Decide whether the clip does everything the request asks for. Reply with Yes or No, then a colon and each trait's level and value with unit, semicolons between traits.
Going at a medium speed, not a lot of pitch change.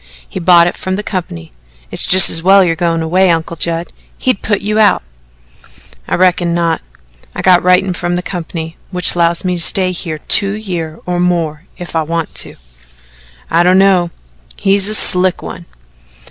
Yes: average, 180 wpm; narrow, 1.9 semitones